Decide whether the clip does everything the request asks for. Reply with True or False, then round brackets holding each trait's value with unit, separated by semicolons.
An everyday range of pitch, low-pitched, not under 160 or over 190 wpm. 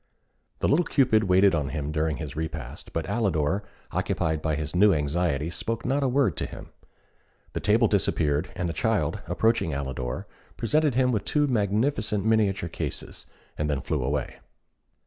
False (6.6 semitones; 90 Hz; 165 wpm)